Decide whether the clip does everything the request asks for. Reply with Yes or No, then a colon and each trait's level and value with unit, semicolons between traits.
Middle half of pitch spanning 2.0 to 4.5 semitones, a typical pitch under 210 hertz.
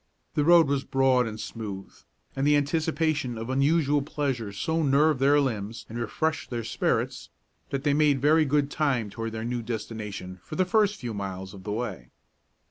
No: average, 4.9 semitones; low, 135 Hz